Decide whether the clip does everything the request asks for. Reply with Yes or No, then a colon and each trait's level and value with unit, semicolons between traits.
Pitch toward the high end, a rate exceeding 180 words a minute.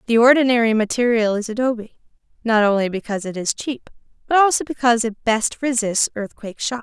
No: high, 230 Hz; average, 165 wpm